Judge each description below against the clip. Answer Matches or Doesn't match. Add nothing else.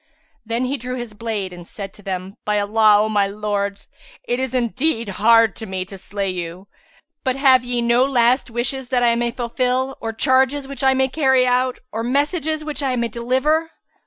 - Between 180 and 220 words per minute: Matches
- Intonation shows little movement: Doesn't match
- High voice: Matches